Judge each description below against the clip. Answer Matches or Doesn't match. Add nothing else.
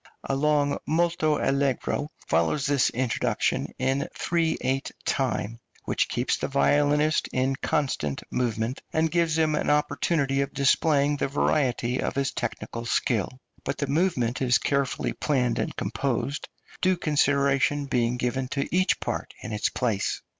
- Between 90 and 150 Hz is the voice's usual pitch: Matches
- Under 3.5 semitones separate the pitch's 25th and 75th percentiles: Matches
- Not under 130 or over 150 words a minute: Matches